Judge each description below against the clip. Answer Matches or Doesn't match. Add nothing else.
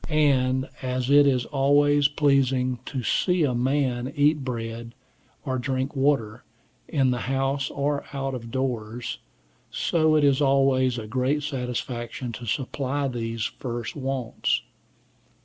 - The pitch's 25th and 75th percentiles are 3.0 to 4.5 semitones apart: Doesn't match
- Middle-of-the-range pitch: Doesn't match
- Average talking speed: Doesn't match